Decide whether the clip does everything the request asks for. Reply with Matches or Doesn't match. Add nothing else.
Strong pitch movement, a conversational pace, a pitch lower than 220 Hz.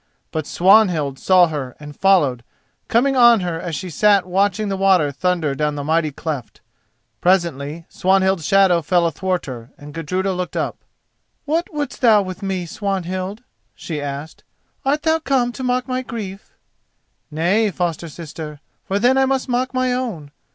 Matches